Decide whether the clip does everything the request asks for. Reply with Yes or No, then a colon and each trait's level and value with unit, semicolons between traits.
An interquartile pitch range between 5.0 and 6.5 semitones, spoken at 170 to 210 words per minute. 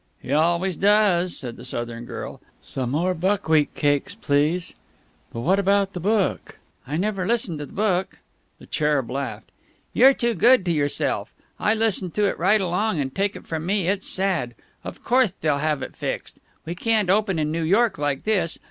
Yes: average, 5.3 semitones; average, 185 wpm